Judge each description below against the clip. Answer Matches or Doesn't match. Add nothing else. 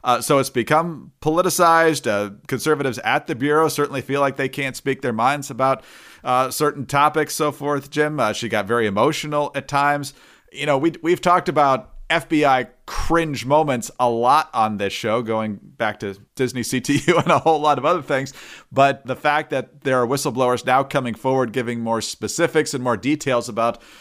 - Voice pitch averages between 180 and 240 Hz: Doesn't match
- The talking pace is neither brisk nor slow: Matches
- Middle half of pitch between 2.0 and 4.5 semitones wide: Matches